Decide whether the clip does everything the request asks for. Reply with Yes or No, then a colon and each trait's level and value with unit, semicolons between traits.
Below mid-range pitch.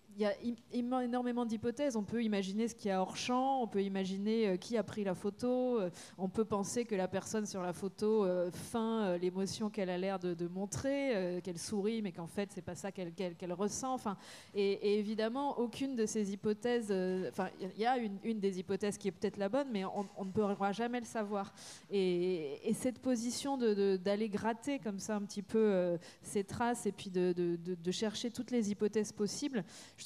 No: high, 205 Hz